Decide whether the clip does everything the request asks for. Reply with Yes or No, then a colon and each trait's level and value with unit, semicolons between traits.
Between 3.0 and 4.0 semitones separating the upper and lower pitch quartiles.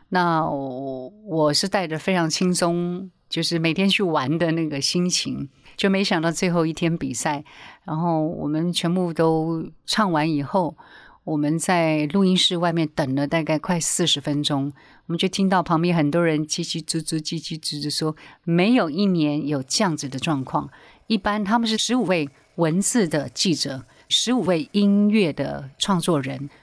Yes: average, 3.3 semitones